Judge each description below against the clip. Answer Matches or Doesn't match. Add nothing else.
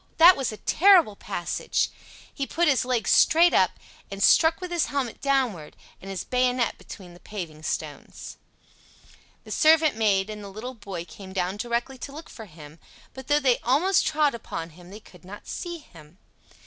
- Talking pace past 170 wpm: Matches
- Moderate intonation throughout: Doesn't match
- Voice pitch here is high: Matches